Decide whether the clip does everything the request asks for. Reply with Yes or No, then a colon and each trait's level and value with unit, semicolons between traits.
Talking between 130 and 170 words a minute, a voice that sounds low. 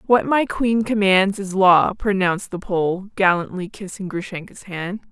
No: average, 150 wpm; high, 195 Hz